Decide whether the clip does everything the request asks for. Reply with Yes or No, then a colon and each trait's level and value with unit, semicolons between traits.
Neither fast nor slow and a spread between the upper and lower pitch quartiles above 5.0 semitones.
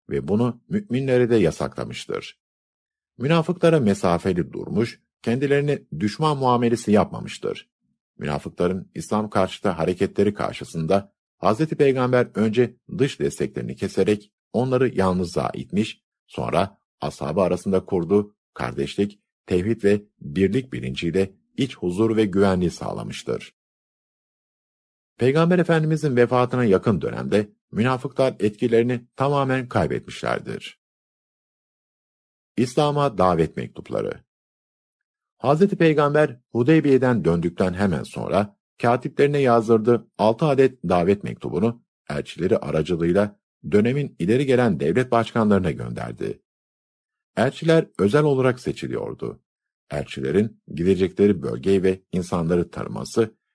No: slow, 90 wpm; wide, 5.6 semitones